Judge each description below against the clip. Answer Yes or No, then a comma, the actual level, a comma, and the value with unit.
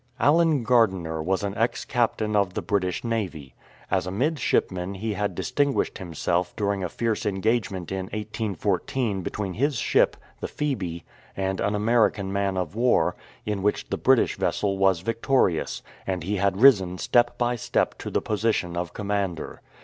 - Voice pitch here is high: No, low, 100 Hz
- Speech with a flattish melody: No, average, 3.7 semitones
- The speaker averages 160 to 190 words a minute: Yes, average, 165 wpm